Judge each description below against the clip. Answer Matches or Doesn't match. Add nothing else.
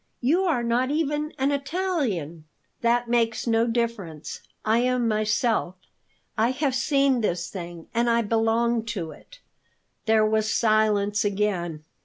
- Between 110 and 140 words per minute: Matches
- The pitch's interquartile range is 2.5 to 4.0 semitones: Matches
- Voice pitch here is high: Matches